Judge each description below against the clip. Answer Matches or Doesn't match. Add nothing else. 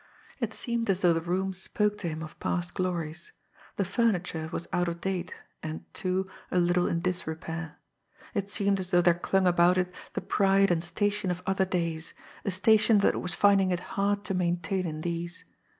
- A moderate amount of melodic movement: Doesn't match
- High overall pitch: Doesn't match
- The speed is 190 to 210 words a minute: Matches